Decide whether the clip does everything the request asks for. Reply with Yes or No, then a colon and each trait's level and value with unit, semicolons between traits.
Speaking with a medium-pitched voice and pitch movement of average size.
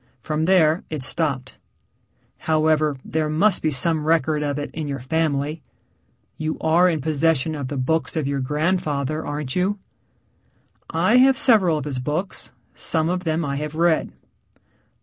No: medium, 155 Hz; narrow, 2.2 semitones